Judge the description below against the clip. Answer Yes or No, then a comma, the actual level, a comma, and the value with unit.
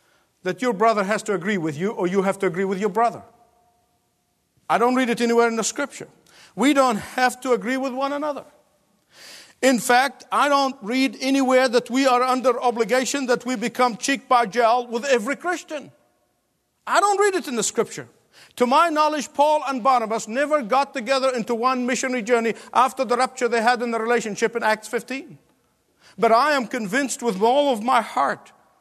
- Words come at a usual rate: Yes, average, 190 wpm